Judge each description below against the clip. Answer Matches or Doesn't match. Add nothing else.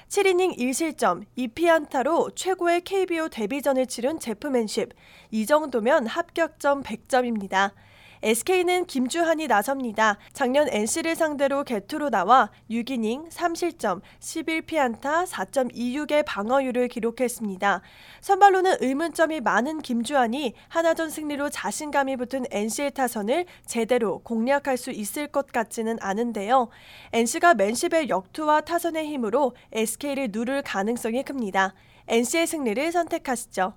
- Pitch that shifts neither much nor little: Doesn't match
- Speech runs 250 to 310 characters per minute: Matches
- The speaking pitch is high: Matches